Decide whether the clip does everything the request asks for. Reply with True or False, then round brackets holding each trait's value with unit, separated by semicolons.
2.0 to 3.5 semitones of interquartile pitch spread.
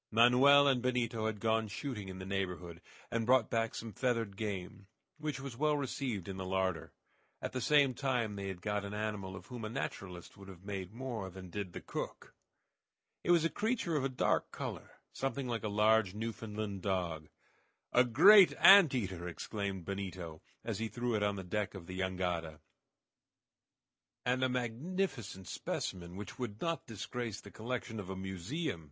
False (4.9 semitones)